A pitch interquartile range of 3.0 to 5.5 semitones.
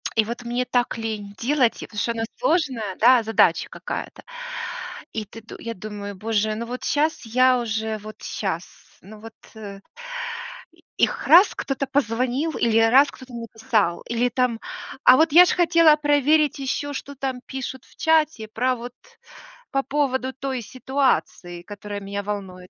Yes: average, 4.0 semitones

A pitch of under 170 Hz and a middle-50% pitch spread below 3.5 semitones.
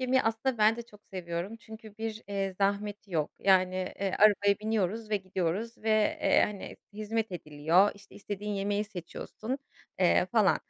No: high, 205 Hz; narrow, 2.6 semitones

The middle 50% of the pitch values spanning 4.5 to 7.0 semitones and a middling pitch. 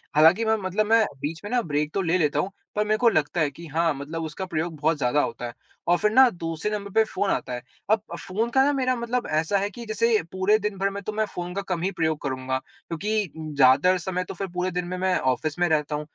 Yes: average, 5.1 semitones; medium, 180 Hz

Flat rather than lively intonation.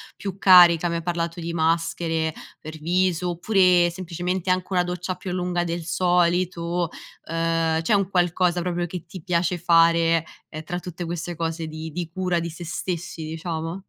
Yes: narrow, 1.4 semitones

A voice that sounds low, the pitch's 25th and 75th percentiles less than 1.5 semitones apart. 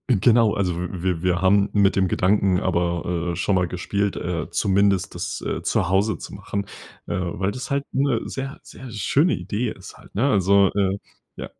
No: low, 100 Hz; average, 2.9 semitones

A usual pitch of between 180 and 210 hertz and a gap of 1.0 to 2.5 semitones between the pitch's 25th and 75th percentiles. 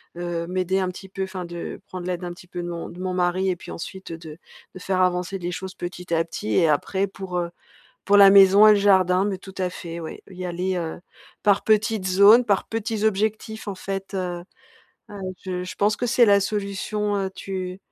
Yes: medium, 185 Hz; narrow, 2.0 semitones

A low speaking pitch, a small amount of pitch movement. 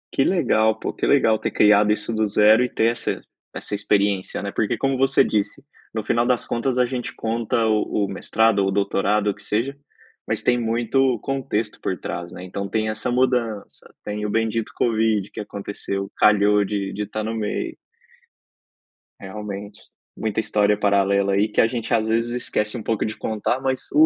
Yes: low, 110 Hz; narrow, 2.1 semitones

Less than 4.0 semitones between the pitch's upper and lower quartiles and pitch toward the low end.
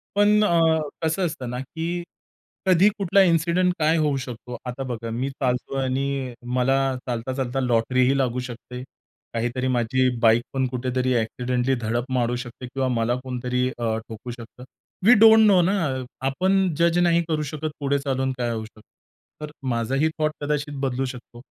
No: average, 4.5 semitones; low, 130 Hz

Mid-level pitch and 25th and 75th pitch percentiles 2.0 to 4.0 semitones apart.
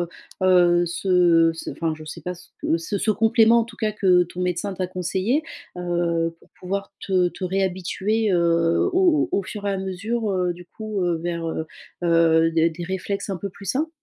Yes: medium, 180 Hz; average, 2.8 semitones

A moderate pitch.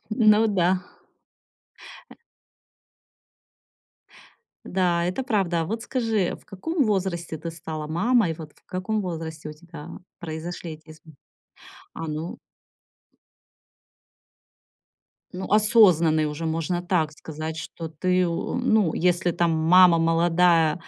Yes: medium, 170 Hz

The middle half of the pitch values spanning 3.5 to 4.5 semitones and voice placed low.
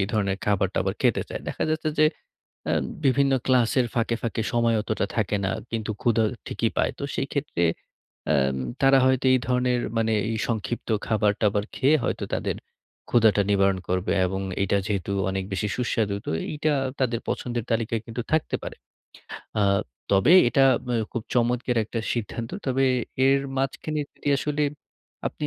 Yes: average, 3.9 semitones; low, 115 Hz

